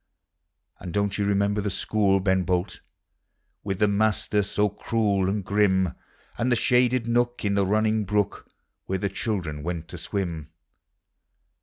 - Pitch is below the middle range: Yes, low, 100 Hz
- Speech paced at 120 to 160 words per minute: Yes, average, 150 wpm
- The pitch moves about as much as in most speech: No, narrow, 2.1 semitones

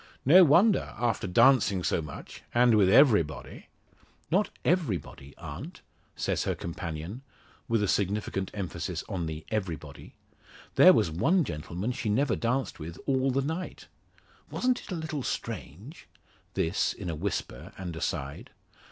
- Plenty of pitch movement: Yes, wide, 8.3 semitones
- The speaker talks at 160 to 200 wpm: No, average, 140 wpm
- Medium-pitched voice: No, low, 105 Hz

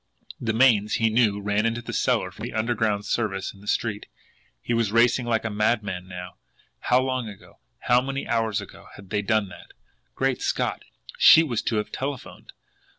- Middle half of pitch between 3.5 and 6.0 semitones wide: No, average, 2.7 semitones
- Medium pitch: No, low, 110 Hz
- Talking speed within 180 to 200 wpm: Yes, average, 185 wpm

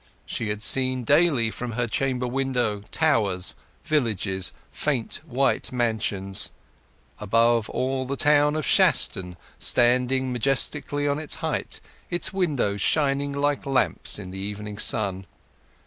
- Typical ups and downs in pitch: Yes, average, 4.9 semitones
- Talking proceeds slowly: Yes, slow, 125 wpm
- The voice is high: No, low, 125 Hz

